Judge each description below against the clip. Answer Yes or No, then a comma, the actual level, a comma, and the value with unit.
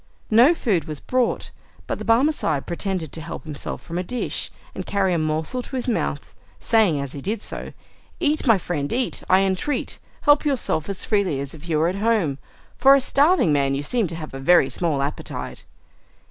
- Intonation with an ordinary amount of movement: No, wide, 7.6 semitones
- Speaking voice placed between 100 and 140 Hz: No, medium, 185 Hz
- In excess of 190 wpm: Yes, average, 200 wpm